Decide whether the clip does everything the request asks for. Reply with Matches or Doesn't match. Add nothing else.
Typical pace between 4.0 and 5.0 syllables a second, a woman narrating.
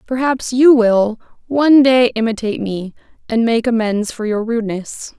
Matches